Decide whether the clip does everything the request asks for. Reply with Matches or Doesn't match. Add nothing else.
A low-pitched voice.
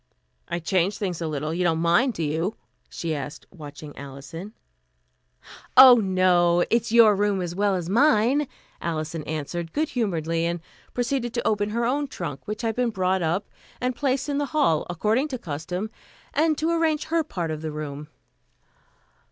Doesn't match